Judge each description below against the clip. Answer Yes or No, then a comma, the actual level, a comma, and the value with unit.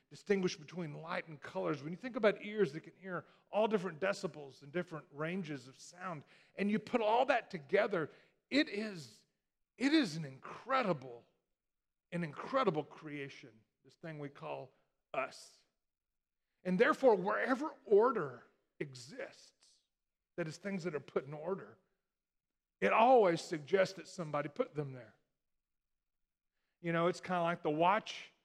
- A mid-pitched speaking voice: Yes, medium, 175 Hz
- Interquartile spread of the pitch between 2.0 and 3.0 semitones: No, average, 4.7 semitones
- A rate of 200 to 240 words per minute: No, average, 150 wpm